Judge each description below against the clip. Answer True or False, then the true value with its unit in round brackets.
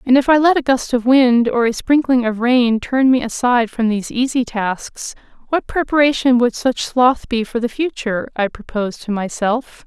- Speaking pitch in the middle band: False (245 Hz)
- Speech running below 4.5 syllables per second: False (4.9 syllables/s)